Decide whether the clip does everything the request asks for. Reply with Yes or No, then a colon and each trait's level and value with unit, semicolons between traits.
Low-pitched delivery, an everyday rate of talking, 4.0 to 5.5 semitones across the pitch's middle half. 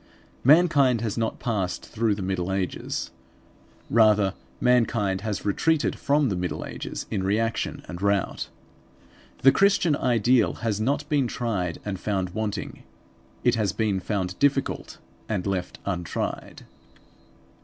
No: low, 110 Hz; slow, 130 wpm; average, 4.4 semitones